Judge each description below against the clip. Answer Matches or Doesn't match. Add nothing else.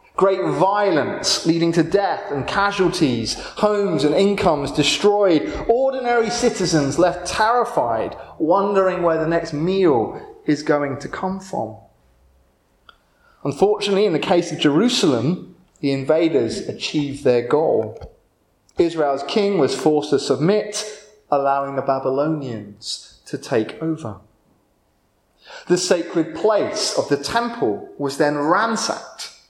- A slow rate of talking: Matches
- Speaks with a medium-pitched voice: Matches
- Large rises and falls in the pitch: Matches